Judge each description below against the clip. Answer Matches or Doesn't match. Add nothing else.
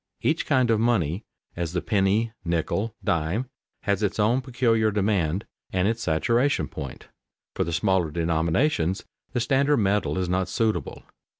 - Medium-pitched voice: Doesn't match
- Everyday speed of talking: Matches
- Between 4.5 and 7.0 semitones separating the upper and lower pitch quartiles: Matches